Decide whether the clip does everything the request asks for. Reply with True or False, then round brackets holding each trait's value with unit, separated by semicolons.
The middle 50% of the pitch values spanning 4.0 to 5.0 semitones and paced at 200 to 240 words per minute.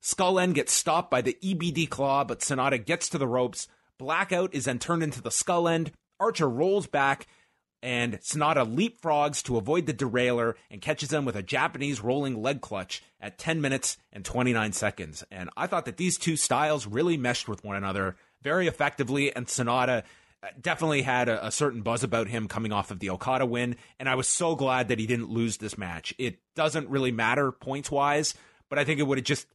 True (4.5 semitones; 205 wpm)